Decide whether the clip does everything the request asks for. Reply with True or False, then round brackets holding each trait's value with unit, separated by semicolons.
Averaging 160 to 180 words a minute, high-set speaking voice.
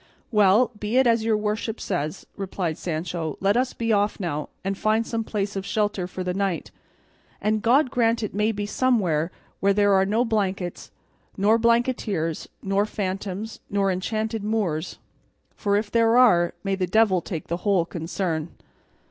True (165 wpm; 205 Hz)